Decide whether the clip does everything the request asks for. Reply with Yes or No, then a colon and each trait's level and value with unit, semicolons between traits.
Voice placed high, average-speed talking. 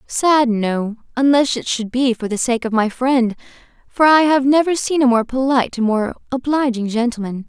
Yes: very high, 250 Hz; average, 195 wpm